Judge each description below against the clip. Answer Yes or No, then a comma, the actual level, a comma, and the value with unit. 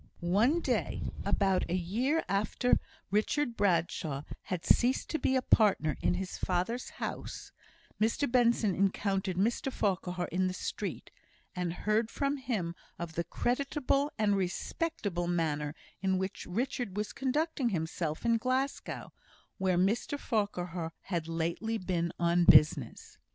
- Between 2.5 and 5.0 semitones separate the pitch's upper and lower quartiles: No, wide, 5.5 semitones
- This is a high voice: Yes, high, 195 Hz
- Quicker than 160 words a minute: No, slow, 135 wpm